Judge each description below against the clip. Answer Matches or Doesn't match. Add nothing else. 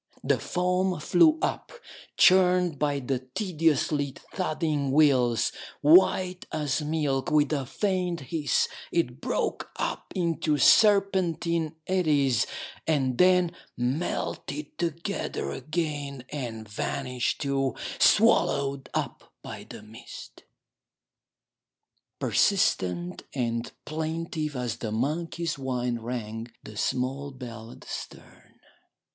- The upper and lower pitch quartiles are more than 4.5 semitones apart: Matches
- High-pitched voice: Doesn't match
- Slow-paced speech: Matches